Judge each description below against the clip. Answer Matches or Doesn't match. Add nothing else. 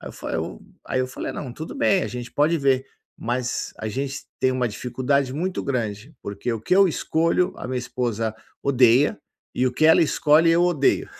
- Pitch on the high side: Doesn't match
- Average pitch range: Matches